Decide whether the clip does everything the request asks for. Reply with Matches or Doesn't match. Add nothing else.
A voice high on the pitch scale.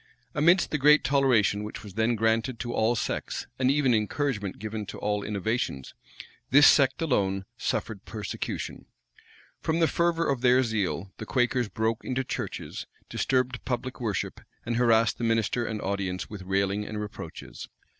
Doesn't match